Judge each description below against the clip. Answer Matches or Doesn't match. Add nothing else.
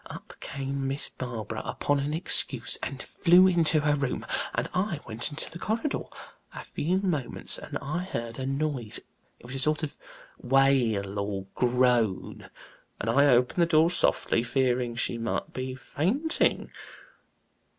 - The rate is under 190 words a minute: Matches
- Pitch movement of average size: Matches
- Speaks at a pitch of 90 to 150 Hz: Matches